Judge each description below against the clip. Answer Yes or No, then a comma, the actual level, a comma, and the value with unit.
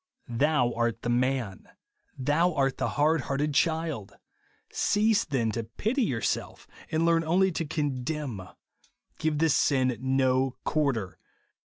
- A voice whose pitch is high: No, medium, 140 Hz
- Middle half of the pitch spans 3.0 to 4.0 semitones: No, average, 4.5 semitones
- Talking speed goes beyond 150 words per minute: No, slow, 135 wpm